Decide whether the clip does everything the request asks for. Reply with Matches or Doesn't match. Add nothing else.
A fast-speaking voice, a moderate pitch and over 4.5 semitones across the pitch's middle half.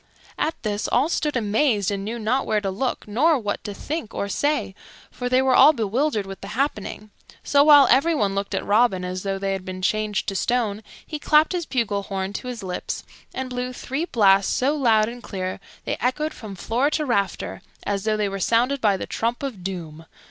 Doesn't match